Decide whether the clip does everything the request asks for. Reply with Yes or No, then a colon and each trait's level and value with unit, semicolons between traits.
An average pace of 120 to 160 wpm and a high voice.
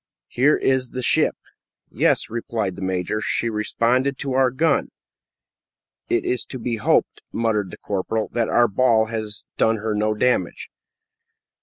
No: average, 150 wpm; low, 115 Hz